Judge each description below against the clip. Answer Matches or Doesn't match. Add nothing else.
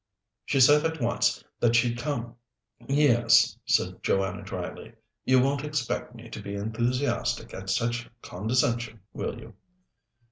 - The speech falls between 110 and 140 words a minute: Matches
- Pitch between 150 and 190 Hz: Doesn't match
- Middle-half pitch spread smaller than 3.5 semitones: Matches